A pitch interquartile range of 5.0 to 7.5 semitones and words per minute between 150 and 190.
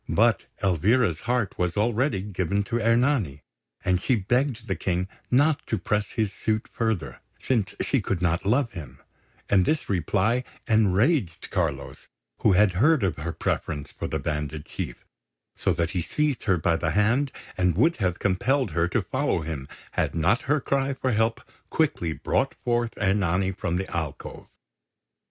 Yes: wide, 5.5 semitones; average, 165 wpm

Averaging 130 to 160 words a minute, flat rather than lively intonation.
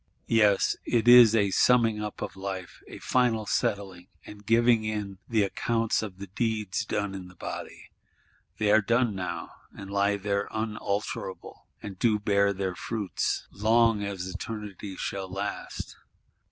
Yes: average, 150 wpm; narrow, 2.3 semitones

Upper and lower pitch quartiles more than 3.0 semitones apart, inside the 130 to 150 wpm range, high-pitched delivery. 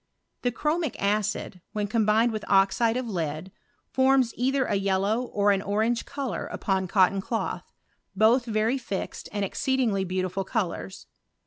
Yes: average, 3.7 semitones; average, 140 wpm; high, 210 Hz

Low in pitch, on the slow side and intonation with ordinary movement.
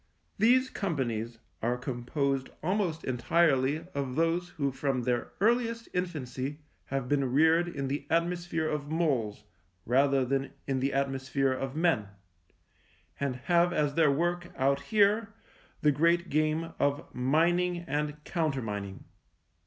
No: medium, 145 Hz; slow, 130 wpm; average, 4.4 semitones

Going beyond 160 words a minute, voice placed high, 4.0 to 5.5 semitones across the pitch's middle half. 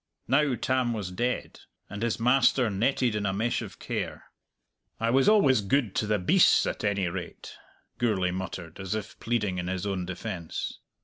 No: average, 175 wpm; low, 105 Hz; average, 4.5 semitones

